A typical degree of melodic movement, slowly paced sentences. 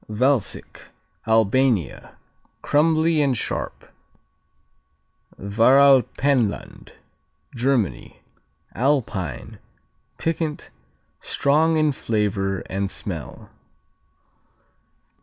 No: wide, 6.1 semitones; slow, 55 wpm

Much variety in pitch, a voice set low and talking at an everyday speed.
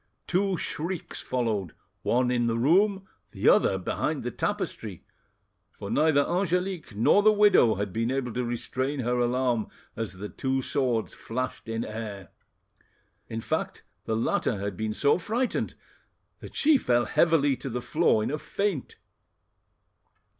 Yes: wide, 6.7 semitones; low, 125 Hz; average, 145 wpm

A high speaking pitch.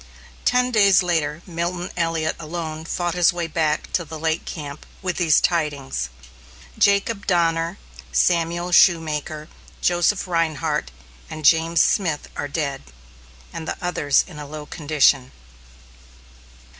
No: medium, 165 Hz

